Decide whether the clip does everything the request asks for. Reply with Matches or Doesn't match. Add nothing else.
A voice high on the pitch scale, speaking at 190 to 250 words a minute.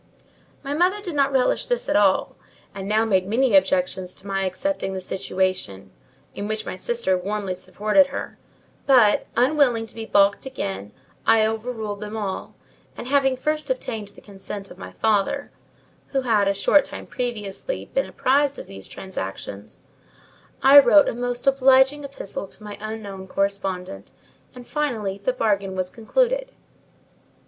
Doesn't match